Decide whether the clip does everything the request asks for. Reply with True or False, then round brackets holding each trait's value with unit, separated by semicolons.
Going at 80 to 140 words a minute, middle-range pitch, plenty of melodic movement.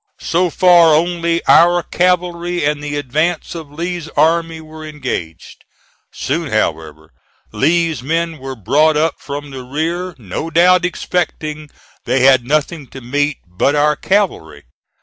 False (135 wpm; 155 Hz; 3.7 semitones)